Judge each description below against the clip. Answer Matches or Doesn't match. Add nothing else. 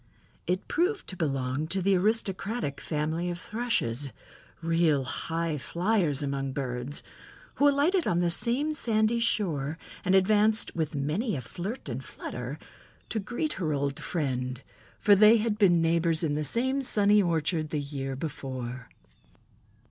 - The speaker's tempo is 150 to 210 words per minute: Doesn't match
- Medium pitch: Matches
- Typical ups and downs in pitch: Doesn't match